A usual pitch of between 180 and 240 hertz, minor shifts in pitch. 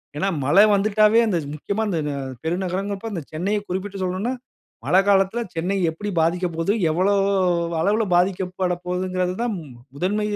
Yes: medium, 185 Hz; narrow, 2.3 semitones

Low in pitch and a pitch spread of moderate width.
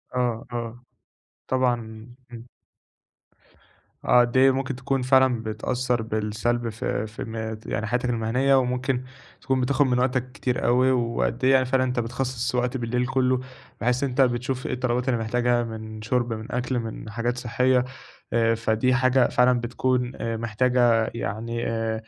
No: low, 125 Hz; narrow, 1.9 semitones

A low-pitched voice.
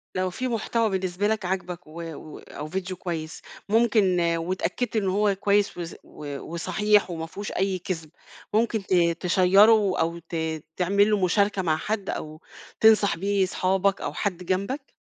No: high, 190 Hz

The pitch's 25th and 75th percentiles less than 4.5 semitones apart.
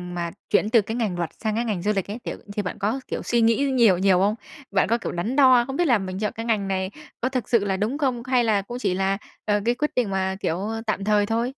Yes: average, 3.7 semitones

